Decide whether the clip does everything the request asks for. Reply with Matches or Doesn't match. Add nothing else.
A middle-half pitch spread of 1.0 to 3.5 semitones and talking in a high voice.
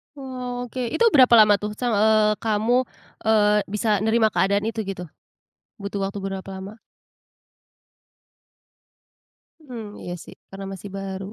Matches